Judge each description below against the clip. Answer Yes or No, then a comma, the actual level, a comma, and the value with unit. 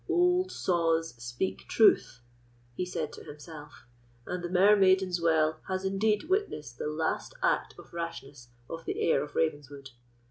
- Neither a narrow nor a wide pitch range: Yes, average, 4.3 semitones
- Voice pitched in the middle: Yes, medium, 165 Hz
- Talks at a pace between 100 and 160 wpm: Yes, average, 145 wpm